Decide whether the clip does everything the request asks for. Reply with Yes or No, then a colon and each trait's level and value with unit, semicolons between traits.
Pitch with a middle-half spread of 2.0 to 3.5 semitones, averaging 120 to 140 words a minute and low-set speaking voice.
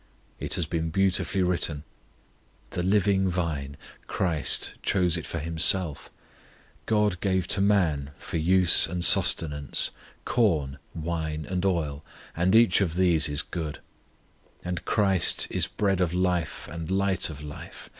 Yes: average, 3.2 semitones; slow, 135 wpm; very low, 85 Hz